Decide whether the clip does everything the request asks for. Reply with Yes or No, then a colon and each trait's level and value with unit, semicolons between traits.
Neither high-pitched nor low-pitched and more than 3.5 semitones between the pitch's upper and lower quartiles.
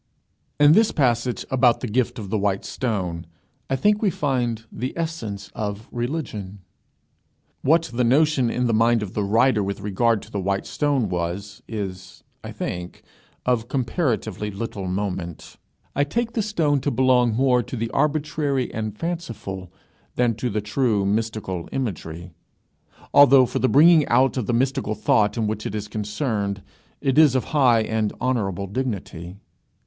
No: low, 115 Hz; average, 4.7 semitones